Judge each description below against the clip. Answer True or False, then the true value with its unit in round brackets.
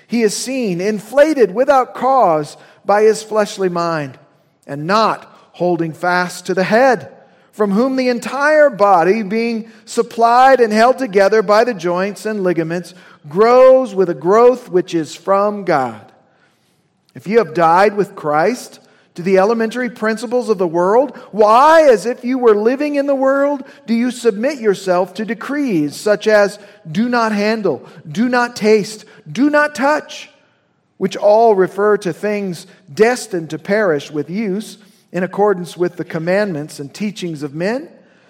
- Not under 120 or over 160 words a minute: True (155 wpm)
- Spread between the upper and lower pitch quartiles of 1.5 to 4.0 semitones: False (4.8 semitones)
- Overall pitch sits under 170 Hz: False (210 Hz)